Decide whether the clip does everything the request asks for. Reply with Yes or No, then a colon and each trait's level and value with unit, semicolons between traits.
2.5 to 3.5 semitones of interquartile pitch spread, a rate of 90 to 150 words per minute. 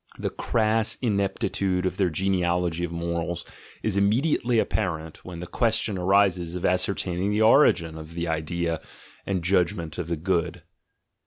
Yes: average, 2.8 semitones; average, 145 wpm